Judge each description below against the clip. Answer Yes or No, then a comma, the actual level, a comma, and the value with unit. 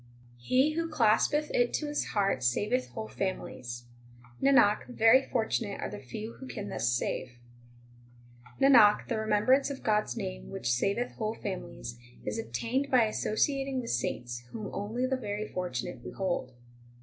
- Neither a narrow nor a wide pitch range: No, wide, 5.9 semitones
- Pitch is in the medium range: No, high, 215 Hz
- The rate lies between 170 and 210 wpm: No, average, 155 wpm